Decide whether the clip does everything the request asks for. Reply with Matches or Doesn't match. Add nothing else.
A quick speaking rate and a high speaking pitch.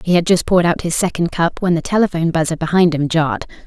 Doesn't match